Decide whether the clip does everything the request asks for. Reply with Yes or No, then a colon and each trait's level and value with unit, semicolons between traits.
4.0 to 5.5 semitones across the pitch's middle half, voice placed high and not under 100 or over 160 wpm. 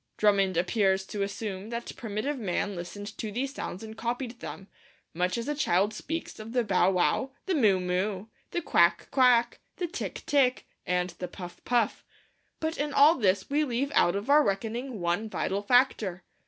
No: average, 5.1 semitones; high, 215 Hz; average, 180 wpm